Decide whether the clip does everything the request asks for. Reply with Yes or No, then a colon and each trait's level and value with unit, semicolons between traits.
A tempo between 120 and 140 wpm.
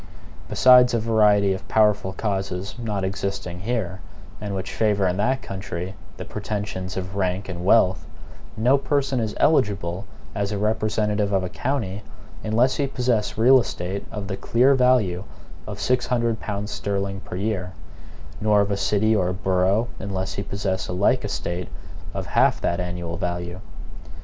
No: average, 160 wpm